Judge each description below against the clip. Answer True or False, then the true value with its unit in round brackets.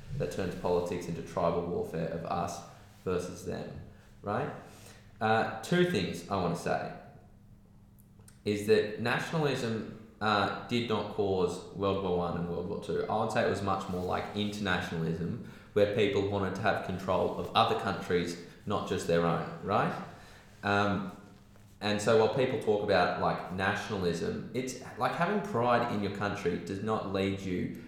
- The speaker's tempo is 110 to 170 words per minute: True (160 wpm)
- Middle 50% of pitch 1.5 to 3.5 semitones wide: True (3.1 semitones)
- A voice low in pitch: True (100 Hz)